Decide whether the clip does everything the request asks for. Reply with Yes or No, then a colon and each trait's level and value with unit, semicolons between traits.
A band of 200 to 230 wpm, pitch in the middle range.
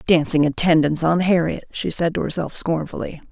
No: average, 165 wpm; medium, 165 Hz